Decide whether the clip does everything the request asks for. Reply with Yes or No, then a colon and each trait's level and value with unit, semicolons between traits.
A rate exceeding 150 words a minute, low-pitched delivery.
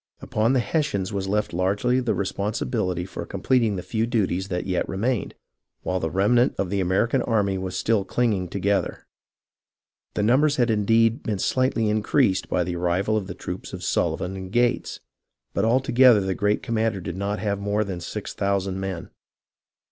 Yes: average, 180 wpm; low, 100 Hz